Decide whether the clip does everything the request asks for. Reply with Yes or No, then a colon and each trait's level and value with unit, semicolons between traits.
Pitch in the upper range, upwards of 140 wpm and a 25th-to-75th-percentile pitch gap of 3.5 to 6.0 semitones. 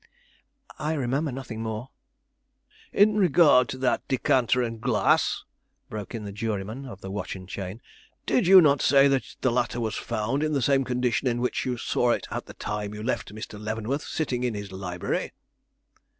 No: low, 120 Hz; average, 180 wpm; average, 4.1 semitones